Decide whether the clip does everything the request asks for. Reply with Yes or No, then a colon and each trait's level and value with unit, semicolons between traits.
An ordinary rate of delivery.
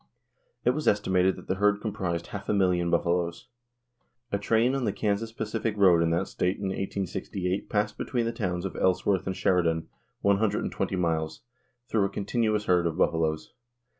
Yes: average, 180 wpm